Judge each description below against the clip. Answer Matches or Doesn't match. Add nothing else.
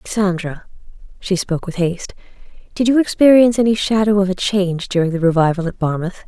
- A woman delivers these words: Matches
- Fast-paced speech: Doesn't match